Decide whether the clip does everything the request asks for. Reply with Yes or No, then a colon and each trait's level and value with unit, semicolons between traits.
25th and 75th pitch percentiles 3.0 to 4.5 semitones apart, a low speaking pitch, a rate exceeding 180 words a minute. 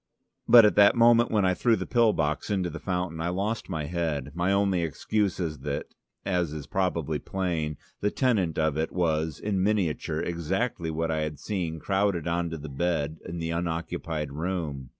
Yes: average, 3.6 semitones; very low, 85 Hz; average, 190 wpm